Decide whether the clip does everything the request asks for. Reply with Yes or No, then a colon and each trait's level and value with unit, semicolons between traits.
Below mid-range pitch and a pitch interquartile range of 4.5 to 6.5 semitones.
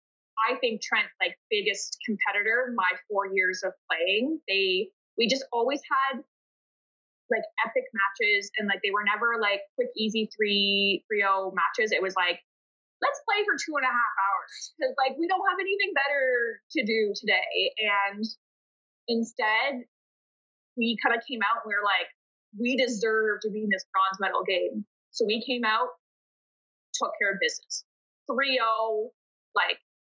No: high, 230 Hz; average, 5.2 semitones